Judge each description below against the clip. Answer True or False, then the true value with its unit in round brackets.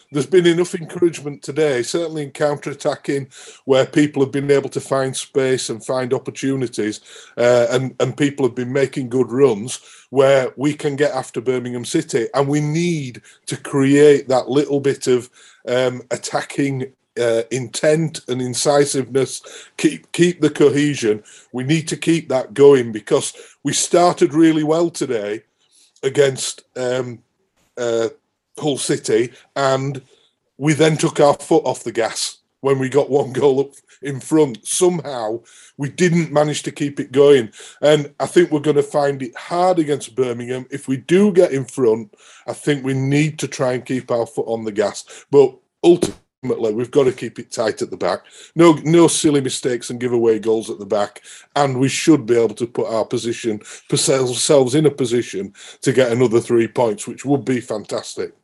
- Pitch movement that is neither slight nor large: True (3.5 semitones)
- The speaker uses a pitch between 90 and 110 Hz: False (140 Hz)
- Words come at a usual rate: True (175 wpm)